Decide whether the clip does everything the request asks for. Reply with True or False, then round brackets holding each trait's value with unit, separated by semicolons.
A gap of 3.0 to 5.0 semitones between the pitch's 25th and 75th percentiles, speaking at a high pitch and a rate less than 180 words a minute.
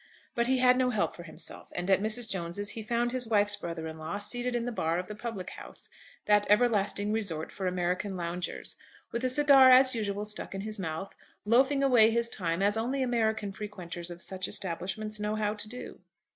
False (4.2 semitones; 210 Hz; 205 wpm)